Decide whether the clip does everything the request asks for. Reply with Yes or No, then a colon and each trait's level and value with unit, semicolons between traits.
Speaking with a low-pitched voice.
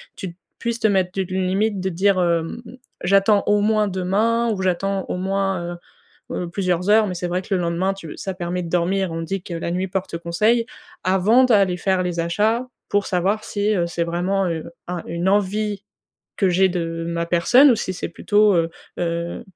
No: high, 190 Hz